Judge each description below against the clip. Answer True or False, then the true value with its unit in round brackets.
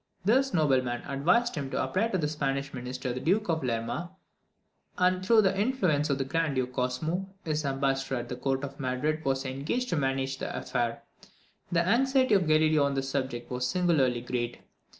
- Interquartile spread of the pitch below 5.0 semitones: False (5.3 semitones)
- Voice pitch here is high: False (140 Hz)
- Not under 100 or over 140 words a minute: False (185 wpm)